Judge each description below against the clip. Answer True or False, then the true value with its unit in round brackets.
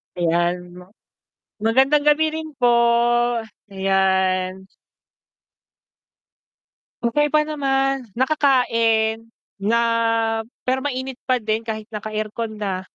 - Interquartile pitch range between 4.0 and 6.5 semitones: True (5.5 semitones)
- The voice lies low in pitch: False (225 Hz)